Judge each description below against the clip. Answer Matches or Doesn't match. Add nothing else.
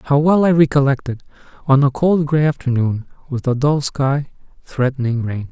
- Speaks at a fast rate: Doesn't match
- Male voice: Matches